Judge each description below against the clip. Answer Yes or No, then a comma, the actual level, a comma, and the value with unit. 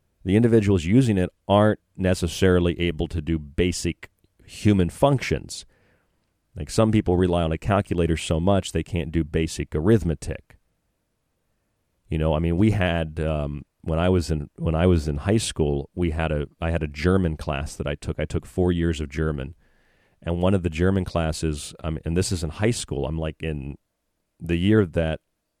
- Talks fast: No, average, 185 wpm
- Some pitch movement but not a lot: Yes, average, 3.2 semitones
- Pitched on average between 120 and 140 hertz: No, very low, 85 Hz